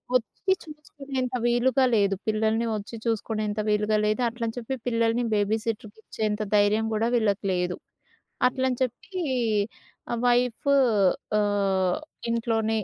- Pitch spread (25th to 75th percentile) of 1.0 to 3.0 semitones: Yes, average, 2.7 semitones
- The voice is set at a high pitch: Yes, high, 225 Hz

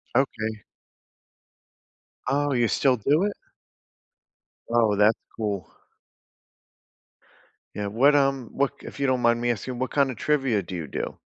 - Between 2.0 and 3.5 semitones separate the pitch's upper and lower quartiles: No, average, 4.1 semitones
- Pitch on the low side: Yes, low, 120 Hz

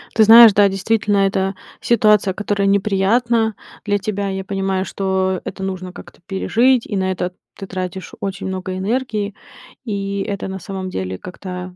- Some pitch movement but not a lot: No, narrow, 1.7 semitones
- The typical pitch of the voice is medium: No, high, 195 Hz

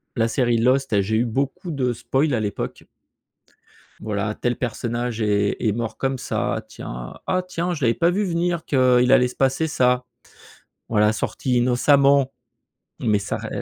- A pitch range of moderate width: Yes, average, 3.9 semitones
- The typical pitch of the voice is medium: No, low, 125 Hz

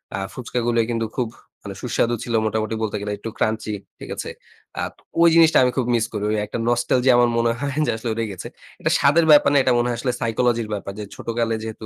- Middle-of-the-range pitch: No, low, 115 Hz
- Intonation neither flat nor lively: No, narrow, 2.1 semitones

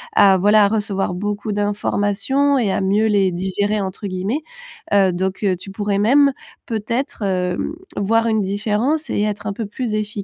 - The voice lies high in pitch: Yes, high, 205 Hz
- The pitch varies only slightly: Yes, narrow, 2.0 semitones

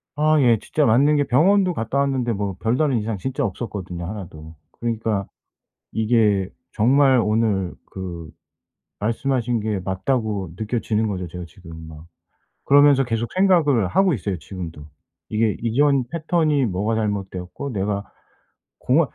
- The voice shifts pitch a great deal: Yes, wide, 5.9 semitones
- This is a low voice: Yes, low, 110 Hz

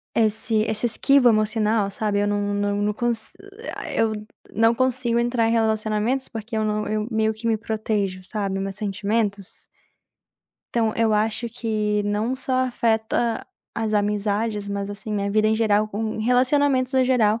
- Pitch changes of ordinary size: No, narrow, 1.8 semitones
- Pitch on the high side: Yes, high, 220 Hz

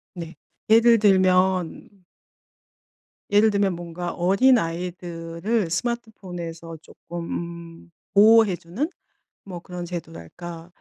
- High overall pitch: No, medium, 180 Hz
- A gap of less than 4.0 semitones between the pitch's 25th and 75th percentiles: Yes, average, 3.3 semitones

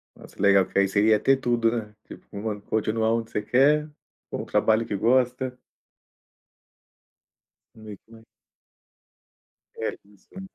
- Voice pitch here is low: Yes, low, 110 Hz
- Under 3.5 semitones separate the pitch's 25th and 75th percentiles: Yes, average, 2.9 semitones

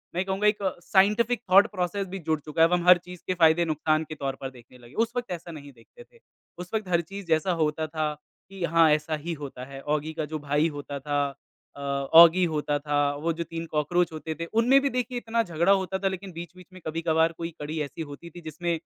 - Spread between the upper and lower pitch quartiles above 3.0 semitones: Yes, average, 3.4 semitones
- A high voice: No, medium, 165 Hz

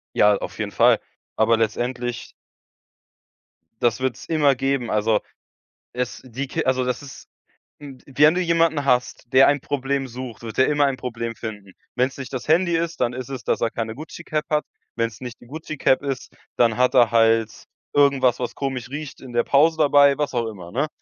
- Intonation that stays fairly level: No, average, 3.4 semitones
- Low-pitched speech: Yes, low, 130 Hz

